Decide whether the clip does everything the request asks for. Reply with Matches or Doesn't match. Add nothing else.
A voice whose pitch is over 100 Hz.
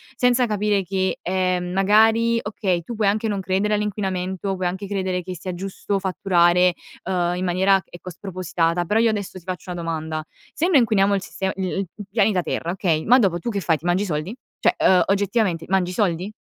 Matches